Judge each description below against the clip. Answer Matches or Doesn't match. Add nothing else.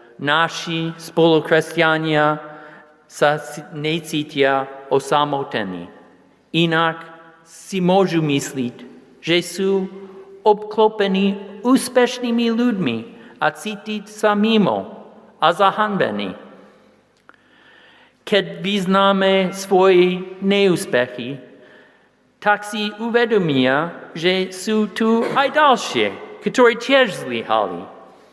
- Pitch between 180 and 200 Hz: Matches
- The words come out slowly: Matches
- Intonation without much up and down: Doesn't match